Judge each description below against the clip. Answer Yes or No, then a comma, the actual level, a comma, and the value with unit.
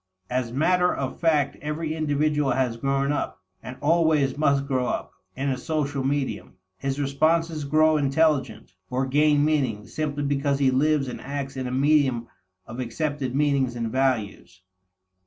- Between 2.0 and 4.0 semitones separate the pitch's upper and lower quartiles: Yes, narrow, 2.6 semitones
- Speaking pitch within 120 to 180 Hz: Yes, medium, 140 Hz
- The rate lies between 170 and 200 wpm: No, average, 155 wpm